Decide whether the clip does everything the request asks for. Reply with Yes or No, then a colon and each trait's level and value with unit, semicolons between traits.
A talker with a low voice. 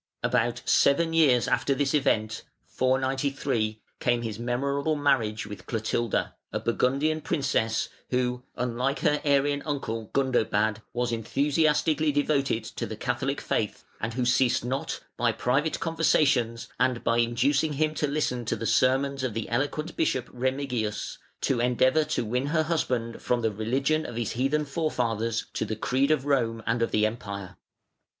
Yes: low, 130 Hz